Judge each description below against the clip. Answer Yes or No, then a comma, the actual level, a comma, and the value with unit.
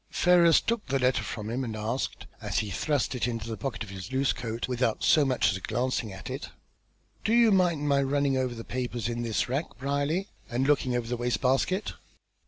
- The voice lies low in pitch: Yes, low, 130 Hz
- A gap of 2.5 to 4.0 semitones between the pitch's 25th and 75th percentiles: Yes, average, 3.5 semitones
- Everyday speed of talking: No, fast, 210 wpm